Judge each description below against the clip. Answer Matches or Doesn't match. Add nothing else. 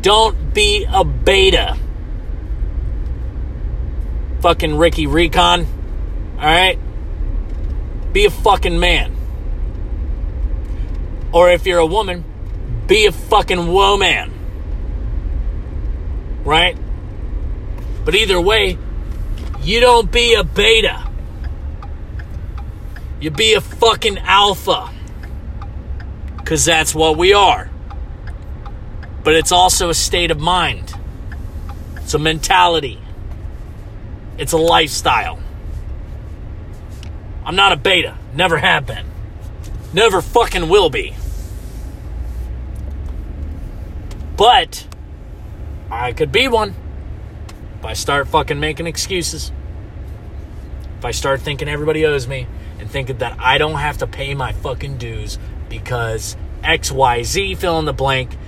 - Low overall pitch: Matches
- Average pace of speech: Doesn't match